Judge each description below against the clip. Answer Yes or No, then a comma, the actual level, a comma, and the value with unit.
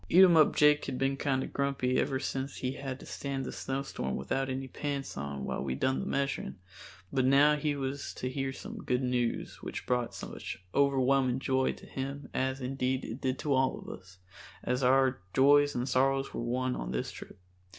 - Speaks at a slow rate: No, average, 190 wpm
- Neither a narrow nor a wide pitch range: No, narrow, 1.4 semitones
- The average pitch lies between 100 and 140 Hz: Yes, low, 135 Hz